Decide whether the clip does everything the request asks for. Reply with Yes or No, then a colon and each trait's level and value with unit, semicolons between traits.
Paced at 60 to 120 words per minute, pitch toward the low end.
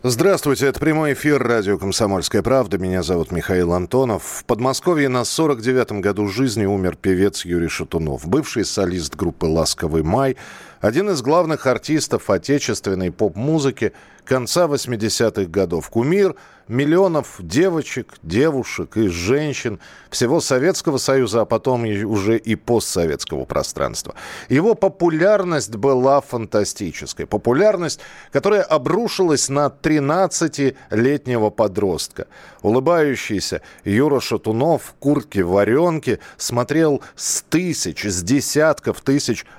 Yes: slow, 110 wpm; low, 130 Hz